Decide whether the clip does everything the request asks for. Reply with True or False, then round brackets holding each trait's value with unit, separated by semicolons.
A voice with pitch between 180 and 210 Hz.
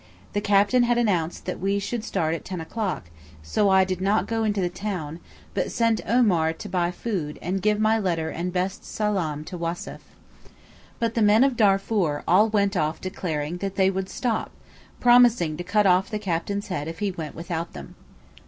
True (190 Hz)